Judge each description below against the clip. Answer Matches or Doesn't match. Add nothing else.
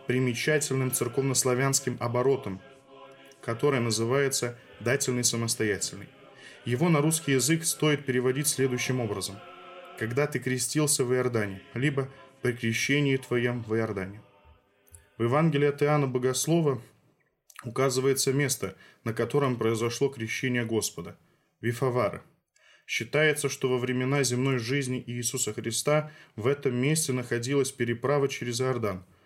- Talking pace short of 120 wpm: Matches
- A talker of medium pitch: Doesn't match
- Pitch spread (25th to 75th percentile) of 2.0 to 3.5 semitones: Matches